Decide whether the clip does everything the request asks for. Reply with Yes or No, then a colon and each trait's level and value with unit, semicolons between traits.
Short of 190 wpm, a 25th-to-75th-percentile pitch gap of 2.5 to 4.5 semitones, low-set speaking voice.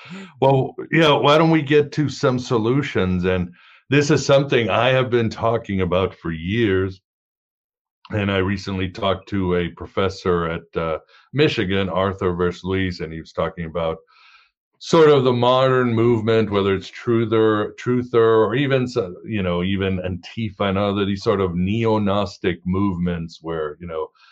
No: average, 160 wpm; wide, 5.5 semitones; low, 100 Hz